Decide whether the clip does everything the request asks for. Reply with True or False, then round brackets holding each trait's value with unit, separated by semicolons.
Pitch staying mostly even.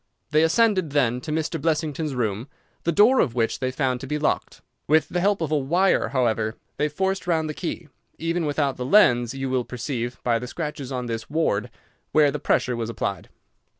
False (4.6 semitones)